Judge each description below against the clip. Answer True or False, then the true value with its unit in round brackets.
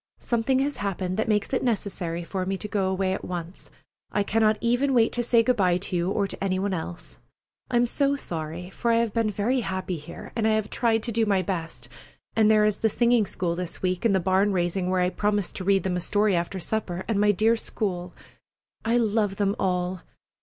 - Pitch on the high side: True (200 Hz)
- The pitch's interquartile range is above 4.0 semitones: False (3.4 semitones)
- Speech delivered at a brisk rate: True (225 wpm)